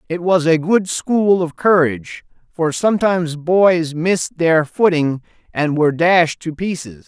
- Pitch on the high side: No, medium, 170 Hz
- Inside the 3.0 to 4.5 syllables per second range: Yes, 4.3 syllables/s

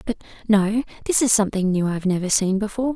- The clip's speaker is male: No, female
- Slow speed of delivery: No, fast, 205 wpm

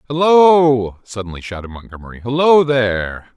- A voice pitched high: No, low, 125 Hz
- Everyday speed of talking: No, slow, 105 wpm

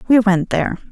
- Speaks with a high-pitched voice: Yes, high, 210 Hz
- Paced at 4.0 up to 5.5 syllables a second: No, 6.2 syllables/s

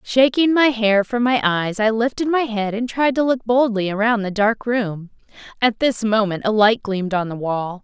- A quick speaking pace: Yes, fast, 215 wpm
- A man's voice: No, female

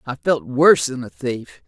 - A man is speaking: Yes, male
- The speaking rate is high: Yes, fast, 215 wpm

